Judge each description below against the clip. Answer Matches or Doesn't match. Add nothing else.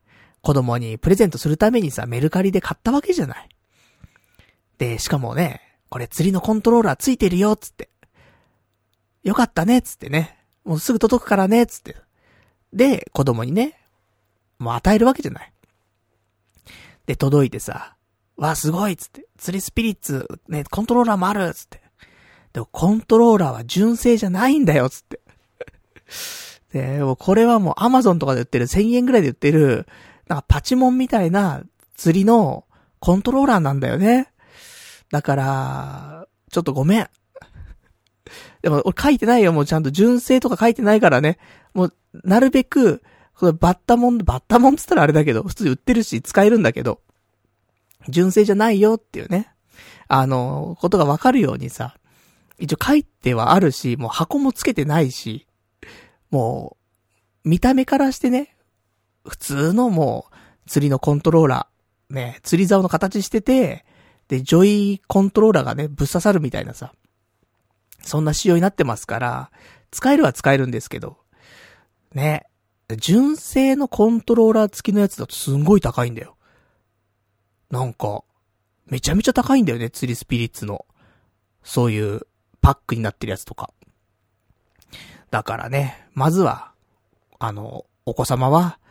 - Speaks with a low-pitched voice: Doesn't match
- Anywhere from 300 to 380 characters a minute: Matches